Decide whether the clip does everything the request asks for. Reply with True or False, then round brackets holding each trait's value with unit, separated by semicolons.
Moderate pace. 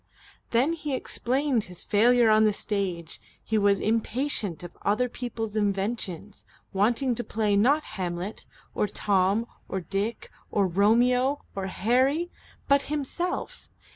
False (130 wpm)